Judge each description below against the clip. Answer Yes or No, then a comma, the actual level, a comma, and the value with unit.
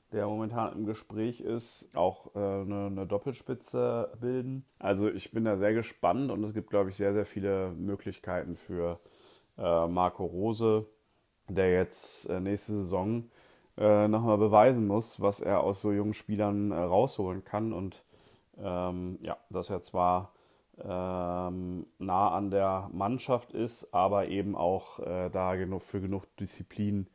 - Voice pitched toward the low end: Yes, low, 100 Hz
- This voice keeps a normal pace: Yes, average, 155 wpm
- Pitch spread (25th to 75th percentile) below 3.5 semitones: Yes, narrow, 2.5 semitones